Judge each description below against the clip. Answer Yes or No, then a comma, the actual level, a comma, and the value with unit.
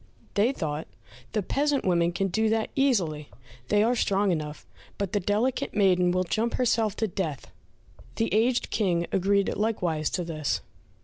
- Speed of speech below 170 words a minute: Yes, average, 160 wpm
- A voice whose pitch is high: Yes, high, 200 Hz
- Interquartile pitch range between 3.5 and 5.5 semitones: Yes, average, 4.4 semitones